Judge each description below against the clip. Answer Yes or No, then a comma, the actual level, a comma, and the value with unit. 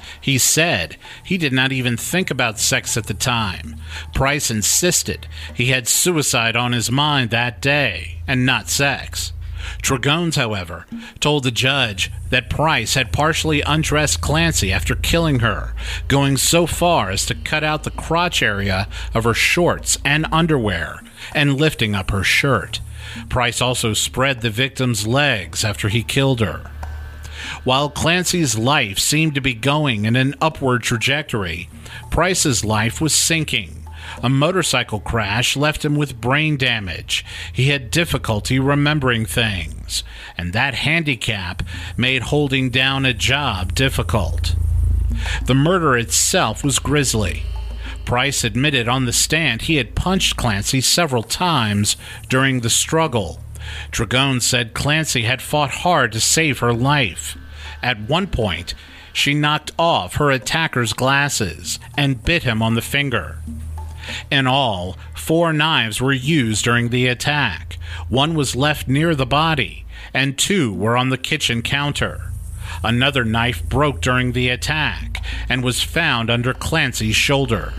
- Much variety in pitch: Yes, wide, 6.5 semitones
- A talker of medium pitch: No, low, 120 Hz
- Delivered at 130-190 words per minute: Yes, average, 140 wpm